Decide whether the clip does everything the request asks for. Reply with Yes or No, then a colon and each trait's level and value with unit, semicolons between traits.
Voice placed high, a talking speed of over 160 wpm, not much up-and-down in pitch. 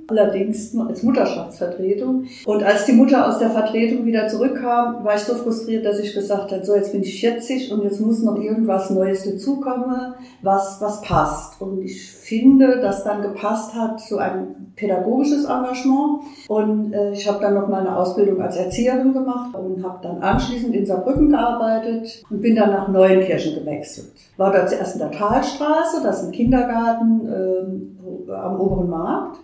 No: high, 215 Hz; average, 175 wpm; average, 4.2 semitones